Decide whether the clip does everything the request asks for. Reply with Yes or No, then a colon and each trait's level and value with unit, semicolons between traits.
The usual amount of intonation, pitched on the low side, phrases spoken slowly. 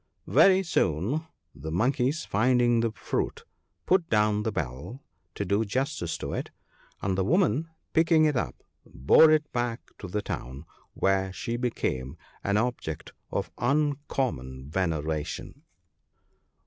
No: wide, 8.2 semitones; low, 115 Hz; slow, 130 wpm